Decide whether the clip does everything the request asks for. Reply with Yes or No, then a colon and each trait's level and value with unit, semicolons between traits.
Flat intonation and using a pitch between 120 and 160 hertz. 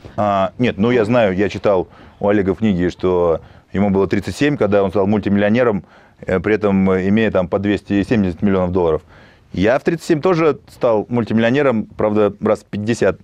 No: narrow, 2.2 semitones; low, 105 Hz